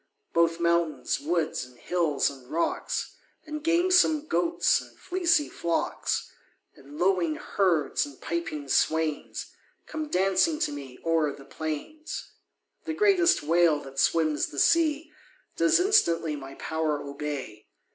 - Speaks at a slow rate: Yes, slow, 125 wpm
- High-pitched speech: No, medium, 165 Hz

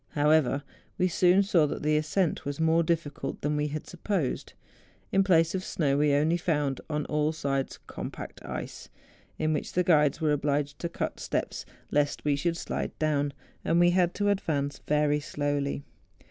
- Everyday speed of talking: Yes, average, 175 wpm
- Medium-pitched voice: Yes, medium, 150 Hz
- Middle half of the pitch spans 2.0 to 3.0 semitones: Yes, average, 2.7 semitones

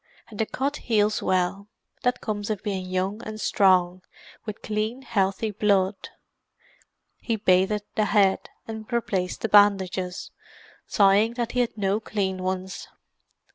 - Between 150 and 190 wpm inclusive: No, slow, 135 wpm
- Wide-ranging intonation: No, narrow, 2.4 semitones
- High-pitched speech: Yes, high, 205 Hz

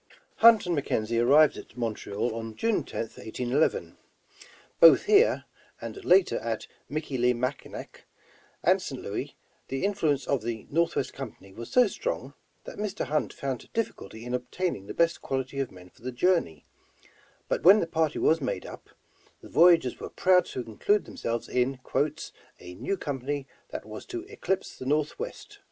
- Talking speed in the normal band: Yes, average, 160 wpm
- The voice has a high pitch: No, medium, 140 Hz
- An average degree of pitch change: No, wide, 7.3 semitones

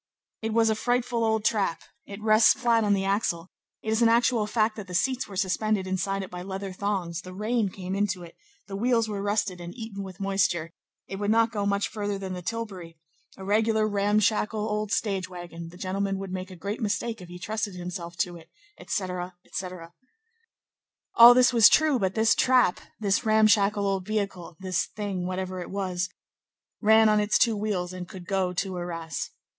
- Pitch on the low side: No, high, 200 Hz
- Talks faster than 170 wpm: Yes, average, 195 wpm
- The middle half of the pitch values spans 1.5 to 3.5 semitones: Yes, average, 2.9 semitones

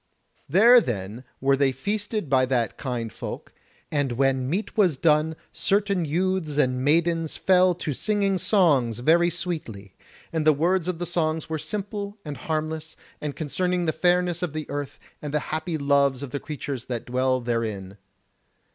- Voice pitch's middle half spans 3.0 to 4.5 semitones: No, average, 5.1 semitones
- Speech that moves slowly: No, average, 165 wpm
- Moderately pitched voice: Yes, medium, 155 Hz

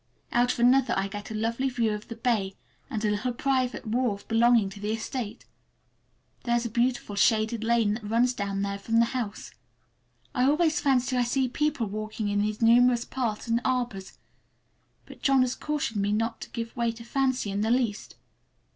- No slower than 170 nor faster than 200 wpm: Yes, average, 190 wpm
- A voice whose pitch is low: No, high, 230 Hz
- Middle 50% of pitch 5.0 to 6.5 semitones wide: No, average, 2.8 semitones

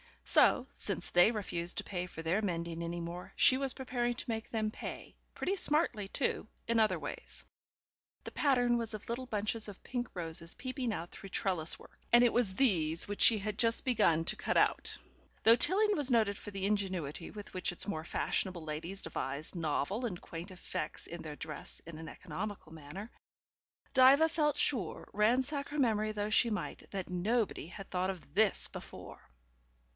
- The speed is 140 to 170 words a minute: No, average, 180 wpm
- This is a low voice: No, high, 205 Hz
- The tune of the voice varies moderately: No, wide, 5.8 semitones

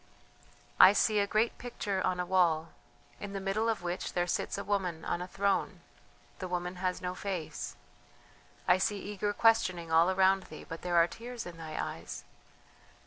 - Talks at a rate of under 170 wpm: No, average, 180 wpm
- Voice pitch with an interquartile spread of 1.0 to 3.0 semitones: Yes, narrow, 2.5 semitones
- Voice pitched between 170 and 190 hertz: Yes, medium, 185 Hz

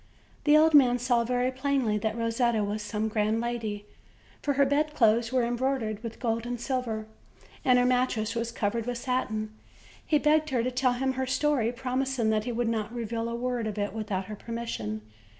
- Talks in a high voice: Yes, high, 235 Hz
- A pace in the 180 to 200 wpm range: Yes, average, 190 wpm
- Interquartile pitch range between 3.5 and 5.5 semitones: No, average, 2.8 semitones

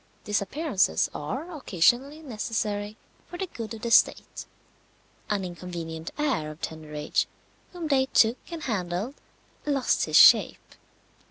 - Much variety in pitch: Yes, wide, 8.0 semitones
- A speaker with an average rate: No, slow, 125 wpm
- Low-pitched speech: No, high, 220 Hz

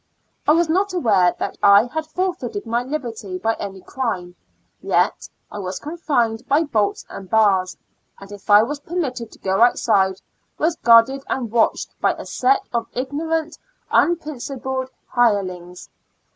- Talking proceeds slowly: No, average, 150 wpm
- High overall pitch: Yes, high, 235 Hz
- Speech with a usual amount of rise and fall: No, wide, 6.4 semitones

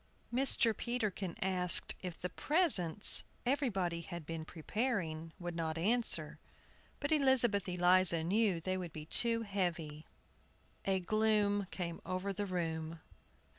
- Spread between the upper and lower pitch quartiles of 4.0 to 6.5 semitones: Yes, average, 4.6 semitones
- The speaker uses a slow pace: Yes, slow, 125 wpm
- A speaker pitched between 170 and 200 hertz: Yes, medium, 185 Hz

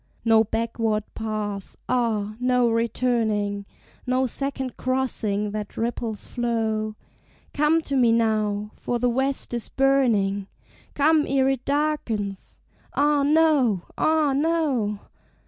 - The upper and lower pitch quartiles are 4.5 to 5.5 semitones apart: No, average, 4.1 semitones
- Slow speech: Yes, slow, 110 wpm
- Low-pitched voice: No, high, 235 Hz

